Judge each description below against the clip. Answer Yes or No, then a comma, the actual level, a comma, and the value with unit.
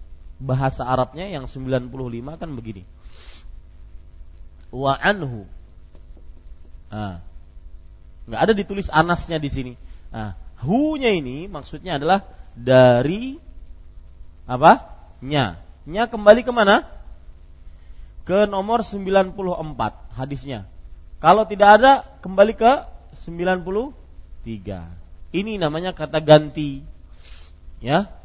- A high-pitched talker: No, low, 125 Hz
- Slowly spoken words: Yes, slow, 85 wpm